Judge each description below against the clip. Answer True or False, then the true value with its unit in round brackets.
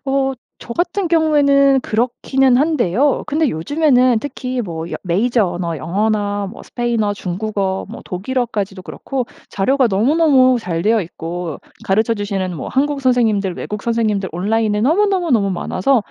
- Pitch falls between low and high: False (230 Hz)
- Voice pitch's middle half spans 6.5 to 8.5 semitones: False (5.6 semitones)